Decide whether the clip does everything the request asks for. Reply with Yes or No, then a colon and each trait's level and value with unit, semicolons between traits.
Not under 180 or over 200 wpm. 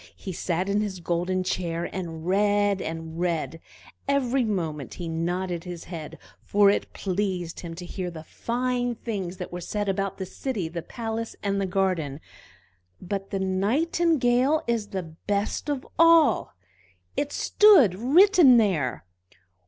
No: average, 145 wpm